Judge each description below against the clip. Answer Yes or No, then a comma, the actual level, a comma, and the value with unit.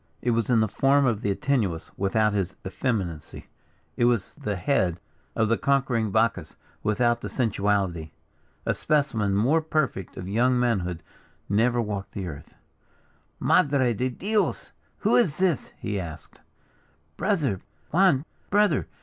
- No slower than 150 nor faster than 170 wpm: No, slow, 135 wpm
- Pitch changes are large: Yes, wide, 5.7 semitones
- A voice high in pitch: No, low, 115 Hz